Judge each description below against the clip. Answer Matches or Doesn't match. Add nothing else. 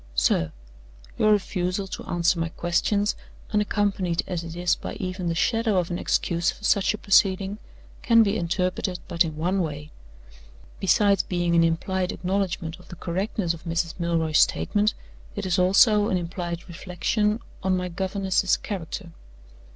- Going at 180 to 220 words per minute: Doesn't match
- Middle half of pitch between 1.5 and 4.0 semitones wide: Matches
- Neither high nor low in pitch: Matches